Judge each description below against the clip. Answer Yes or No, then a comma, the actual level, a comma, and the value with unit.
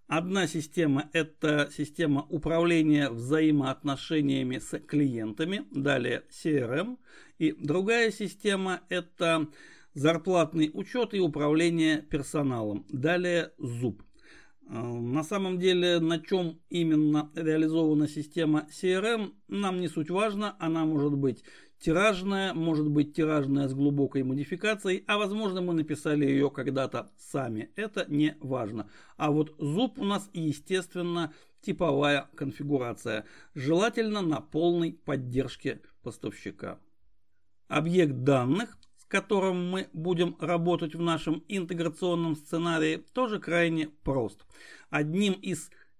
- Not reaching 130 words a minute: Yes, slow, 110 wpm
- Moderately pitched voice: Yes, medium, 160 Hz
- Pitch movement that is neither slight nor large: Yes, average, 3.6 semitones